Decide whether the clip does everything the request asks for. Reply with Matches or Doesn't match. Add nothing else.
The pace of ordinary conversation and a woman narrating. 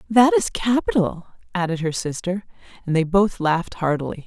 Matches